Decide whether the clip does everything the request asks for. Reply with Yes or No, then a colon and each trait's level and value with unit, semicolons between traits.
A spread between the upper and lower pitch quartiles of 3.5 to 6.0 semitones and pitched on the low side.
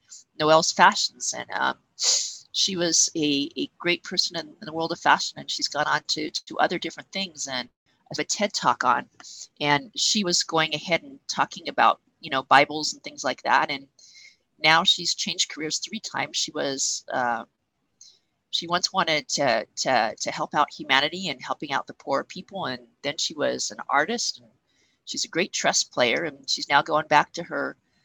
No: average, 4.2 semitones; medium, 160 Hz